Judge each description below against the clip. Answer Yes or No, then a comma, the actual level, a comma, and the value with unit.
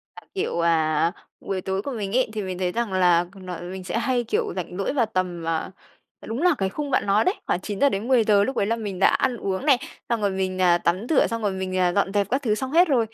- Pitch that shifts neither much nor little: Yes, average, 4.3 semitones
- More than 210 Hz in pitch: No, high, 200 Hz